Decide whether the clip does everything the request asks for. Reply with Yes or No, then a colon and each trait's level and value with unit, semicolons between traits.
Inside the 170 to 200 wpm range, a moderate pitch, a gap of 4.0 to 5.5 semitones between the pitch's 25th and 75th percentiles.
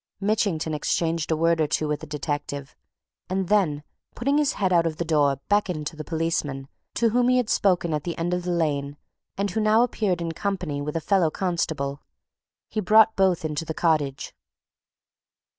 Yes: average, 190 wpm; medium, 165 Hz; average, 4.5 semitones